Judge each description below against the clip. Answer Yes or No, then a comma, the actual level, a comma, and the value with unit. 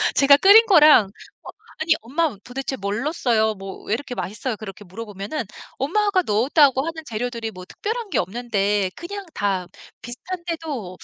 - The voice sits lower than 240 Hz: No, high, 245 Hz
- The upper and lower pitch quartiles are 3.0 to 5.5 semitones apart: No, wide, 7.5 semitones